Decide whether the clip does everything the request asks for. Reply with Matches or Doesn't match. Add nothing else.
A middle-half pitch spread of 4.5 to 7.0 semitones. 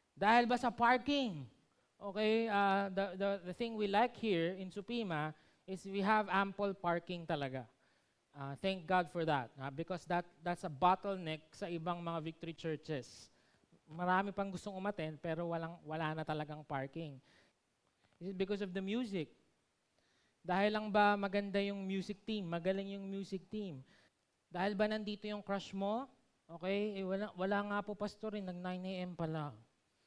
Doesn't match